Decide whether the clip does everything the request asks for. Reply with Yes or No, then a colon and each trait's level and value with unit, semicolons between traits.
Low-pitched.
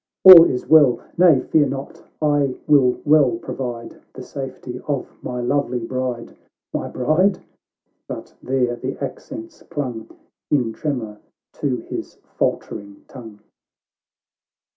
Yes: low, 130 Hz